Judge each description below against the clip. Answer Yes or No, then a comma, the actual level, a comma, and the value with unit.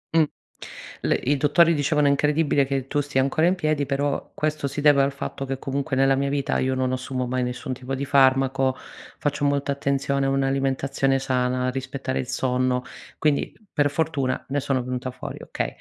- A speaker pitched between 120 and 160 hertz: Yes, low, 135 Hz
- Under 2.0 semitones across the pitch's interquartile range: Yes, narrow, 1.6 semitones